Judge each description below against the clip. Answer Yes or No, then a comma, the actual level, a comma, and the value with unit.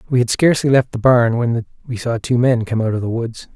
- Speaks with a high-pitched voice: No, low, 120 Hz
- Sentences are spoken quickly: Yes, fast, 270 wpm